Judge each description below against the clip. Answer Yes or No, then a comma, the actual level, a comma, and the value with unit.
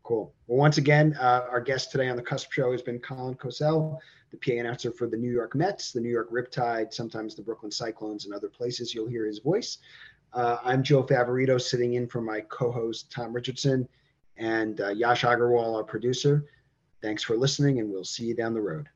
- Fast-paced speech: Yes, fast, 210 wpm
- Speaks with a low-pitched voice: Yes, low, 120 Hz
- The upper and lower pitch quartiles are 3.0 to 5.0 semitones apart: No, narrow, 2.5 semitones